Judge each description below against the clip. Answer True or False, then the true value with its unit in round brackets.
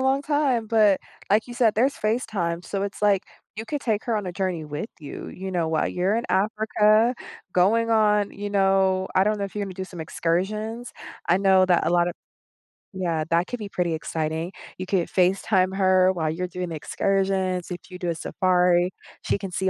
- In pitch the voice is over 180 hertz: True (190 Hz)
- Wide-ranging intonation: False (3.1 semitones)